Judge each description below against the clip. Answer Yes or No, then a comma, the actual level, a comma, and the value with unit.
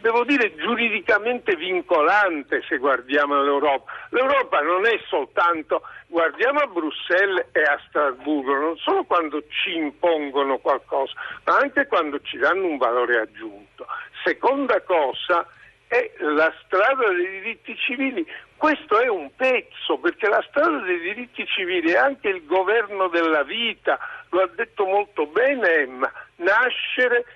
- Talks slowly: No, average, 135 wpm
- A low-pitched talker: No, high, 245 Hz